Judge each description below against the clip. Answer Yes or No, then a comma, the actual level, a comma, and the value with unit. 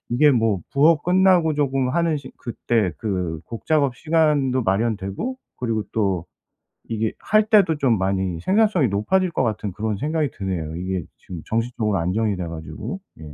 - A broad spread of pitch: Yes, wide, 8.0 semitones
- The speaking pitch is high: No, low, 115 Hz